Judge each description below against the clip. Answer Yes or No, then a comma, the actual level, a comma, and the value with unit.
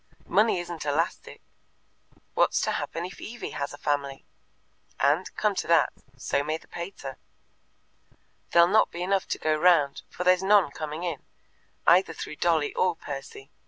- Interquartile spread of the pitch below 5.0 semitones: Yes, average, 3.8 semitones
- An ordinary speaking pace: Yes, average, 160 wpm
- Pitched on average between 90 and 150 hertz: No, medium, 170 Hz